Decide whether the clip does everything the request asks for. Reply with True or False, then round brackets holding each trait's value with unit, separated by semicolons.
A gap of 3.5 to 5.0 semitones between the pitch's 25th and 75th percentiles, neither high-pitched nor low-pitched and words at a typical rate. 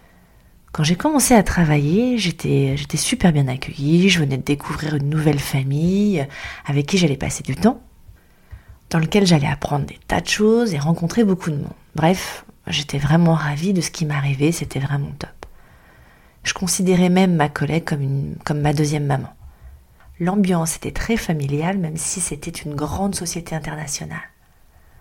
True (3.9 semitones; 155 Hz; 165 wpm)